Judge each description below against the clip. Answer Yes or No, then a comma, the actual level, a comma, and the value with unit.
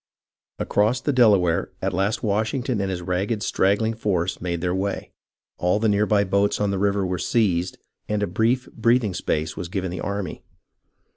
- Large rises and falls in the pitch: No, average, 3.1 semitones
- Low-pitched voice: Yes, low, 100 Hz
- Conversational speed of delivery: Yes, average, 175 wpm